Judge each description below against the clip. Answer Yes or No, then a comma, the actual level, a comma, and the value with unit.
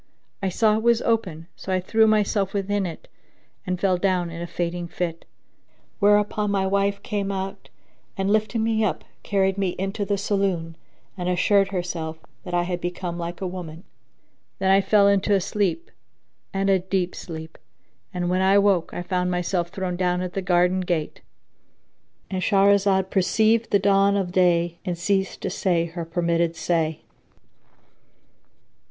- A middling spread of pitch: No, narrow, 2.2 semitones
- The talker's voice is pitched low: No, high, 190 Hz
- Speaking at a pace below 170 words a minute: Yes, average, 160 wpm